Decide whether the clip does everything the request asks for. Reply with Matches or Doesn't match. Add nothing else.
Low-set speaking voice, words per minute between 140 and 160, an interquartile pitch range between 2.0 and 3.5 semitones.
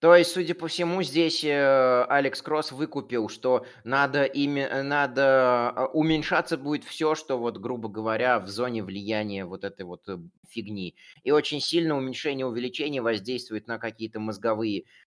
Doesn't match